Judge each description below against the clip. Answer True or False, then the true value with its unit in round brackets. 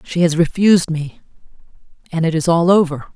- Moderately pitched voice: True (165 Hz)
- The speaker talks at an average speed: True (170 wpm)